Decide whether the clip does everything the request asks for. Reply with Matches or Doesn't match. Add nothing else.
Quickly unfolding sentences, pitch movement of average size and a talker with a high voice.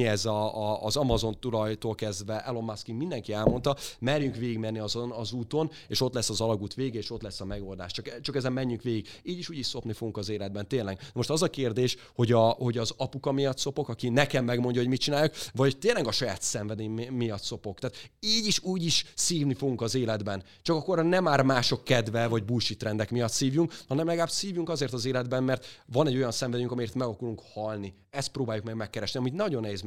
Doesn't match